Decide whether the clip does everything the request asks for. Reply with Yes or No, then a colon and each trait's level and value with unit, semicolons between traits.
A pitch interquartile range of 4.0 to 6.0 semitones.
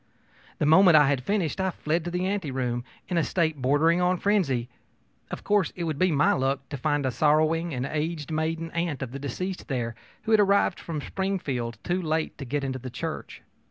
Yes: average, 4.6 semitones